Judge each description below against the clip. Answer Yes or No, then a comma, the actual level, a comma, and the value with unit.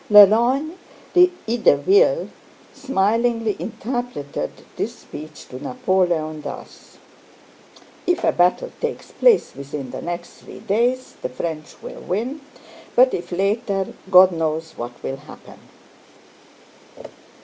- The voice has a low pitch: No, high, 205 Hz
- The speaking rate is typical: No, slow, 105 wpm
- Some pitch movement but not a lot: No, wide, 8.0 semitones